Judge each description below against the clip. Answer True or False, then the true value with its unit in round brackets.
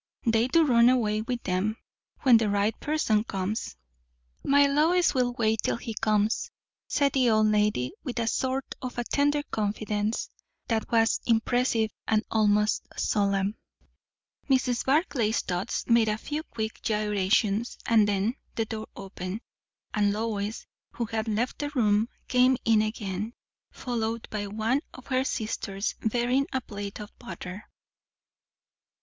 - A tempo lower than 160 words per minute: True (140 wpm)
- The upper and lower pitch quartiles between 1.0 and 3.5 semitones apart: True (2.9 semitones)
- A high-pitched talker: True (220 Hz)